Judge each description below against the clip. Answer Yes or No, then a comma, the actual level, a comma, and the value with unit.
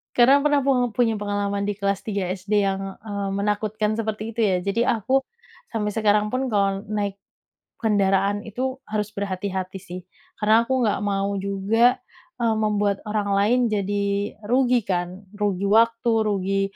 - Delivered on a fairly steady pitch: Yes, narrow, 2.2 semitones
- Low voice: No, high, 210 Hz